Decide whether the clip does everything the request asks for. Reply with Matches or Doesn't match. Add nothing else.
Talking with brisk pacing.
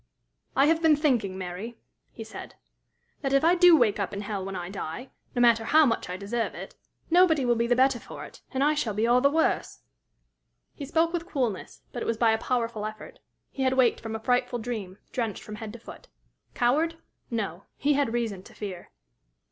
Matches